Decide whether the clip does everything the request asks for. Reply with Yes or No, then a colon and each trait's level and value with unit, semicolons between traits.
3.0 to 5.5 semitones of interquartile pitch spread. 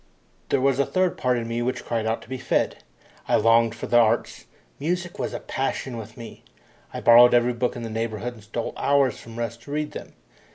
No: narrow, 2.4 semitones